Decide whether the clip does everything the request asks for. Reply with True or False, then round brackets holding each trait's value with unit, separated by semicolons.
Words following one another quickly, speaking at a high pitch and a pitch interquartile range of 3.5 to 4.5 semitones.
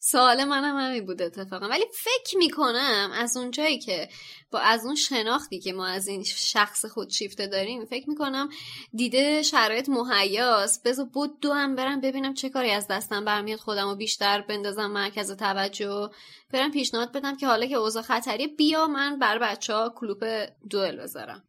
False (175 wpm; 230 Hz; 5.0 semitones)